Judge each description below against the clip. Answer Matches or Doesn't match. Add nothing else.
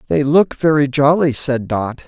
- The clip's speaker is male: Matches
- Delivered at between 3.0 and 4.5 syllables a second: Matches